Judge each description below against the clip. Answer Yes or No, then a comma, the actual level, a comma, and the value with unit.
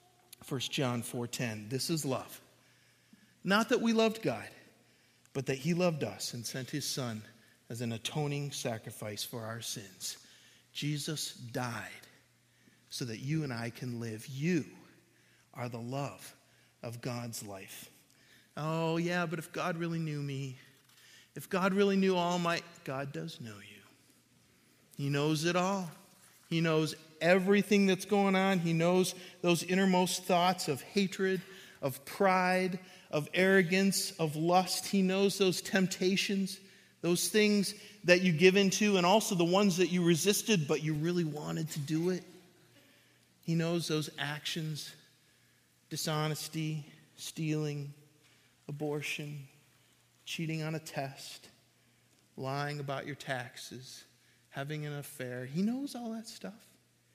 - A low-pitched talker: No, medium, 155 Hz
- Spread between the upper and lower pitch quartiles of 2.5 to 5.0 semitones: No, wide, 5.4 semitones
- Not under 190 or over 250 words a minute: No, average, 140 wpm